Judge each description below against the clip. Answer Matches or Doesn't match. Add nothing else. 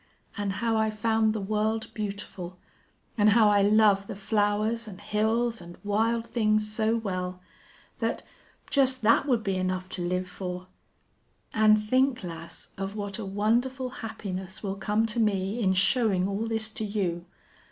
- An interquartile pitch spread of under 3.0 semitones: Matches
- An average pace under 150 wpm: Doesn't match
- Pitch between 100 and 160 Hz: Doesn't match